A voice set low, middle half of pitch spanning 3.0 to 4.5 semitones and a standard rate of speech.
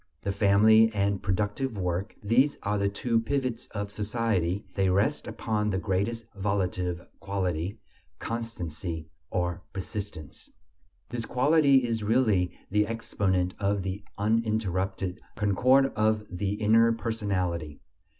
No: low, 100 Hz; average, 3.3 semitones; slow, 120 wpm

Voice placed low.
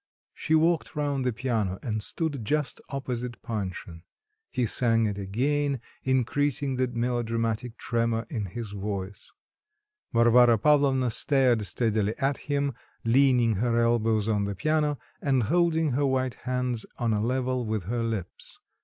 Yes: low, 120 Hz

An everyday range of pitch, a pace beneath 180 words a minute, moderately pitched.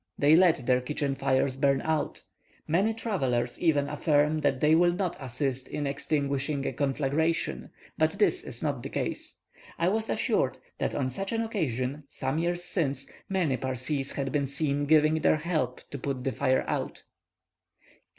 Yes: average, 3.4 semitones; average, 165 wpm; medium, 145 Hz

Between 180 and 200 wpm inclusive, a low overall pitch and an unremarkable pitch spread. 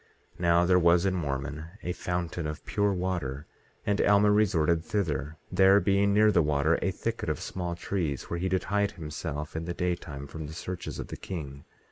Yes: average, 195 wpm; very low, 85 Hz; average, 3.8 semitones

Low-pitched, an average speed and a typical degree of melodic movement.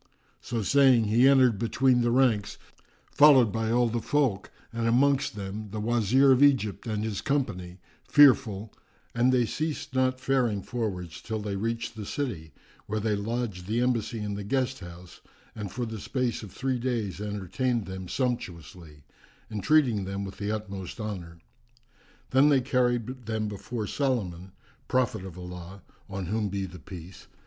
Yes: low, 110 Hz; average, 160 wpm; average, 4.5 semitones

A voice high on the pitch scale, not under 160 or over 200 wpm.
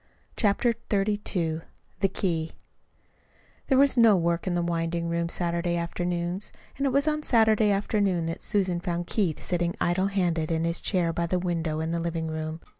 No: medium, 175 Hz; average, 175 wpm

